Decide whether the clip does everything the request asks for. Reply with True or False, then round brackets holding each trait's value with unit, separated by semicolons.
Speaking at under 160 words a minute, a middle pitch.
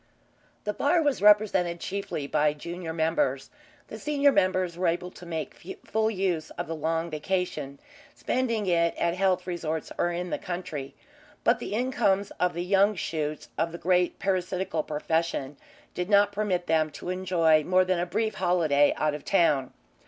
False (165 wpm; 180 Hz)